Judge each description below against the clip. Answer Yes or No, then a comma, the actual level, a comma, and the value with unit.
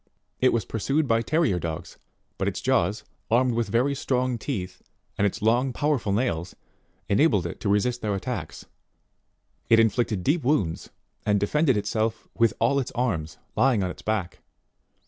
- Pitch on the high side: No, low, 115 Hz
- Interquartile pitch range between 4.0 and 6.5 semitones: Yes, average, 4.3 semitones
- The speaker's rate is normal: Yes, average, 165 wpm